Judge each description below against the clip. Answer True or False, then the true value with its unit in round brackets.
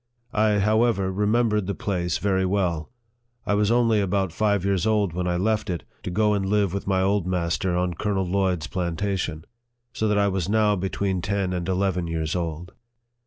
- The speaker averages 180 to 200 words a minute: True (185 wpm)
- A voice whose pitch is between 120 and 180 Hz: False (95 Hz)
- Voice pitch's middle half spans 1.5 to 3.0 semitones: True (2.5 semitones)